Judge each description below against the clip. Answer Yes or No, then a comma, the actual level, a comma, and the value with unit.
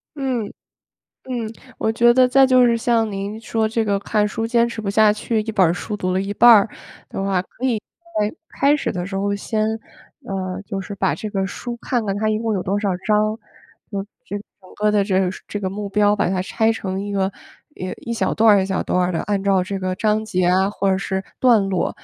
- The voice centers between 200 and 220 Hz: Yes, high, 210 Hz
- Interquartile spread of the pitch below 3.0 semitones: Yes, narrow, 2.6 semitones